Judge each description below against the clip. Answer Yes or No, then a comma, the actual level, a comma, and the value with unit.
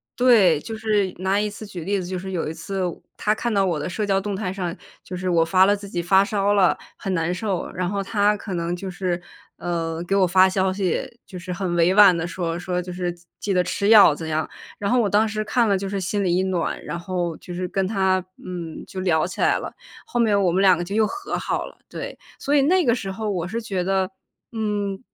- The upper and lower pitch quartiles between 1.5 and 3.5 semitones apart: Yes, narrow, 2.5 semitones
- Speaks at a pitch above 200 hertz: No, high, 190 Hz